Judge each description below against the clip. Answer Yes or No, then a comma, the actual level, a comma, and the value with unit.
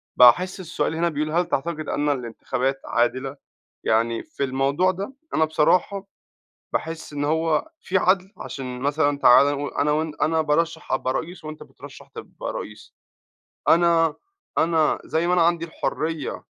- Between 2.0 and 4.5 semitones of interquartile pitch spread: Yes, average, 3.3 semitones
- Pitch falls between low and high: Yes, medium, 155 Hz